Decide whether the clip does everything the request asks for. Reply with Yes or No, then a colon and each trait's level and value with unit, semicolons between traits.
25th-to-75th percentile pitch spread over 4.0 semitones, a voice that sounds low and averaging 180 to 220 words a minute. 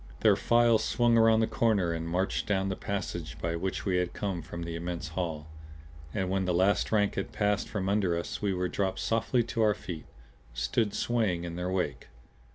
No: average, 3.6 semitones; very low, 95 Hz; average, 200 wpm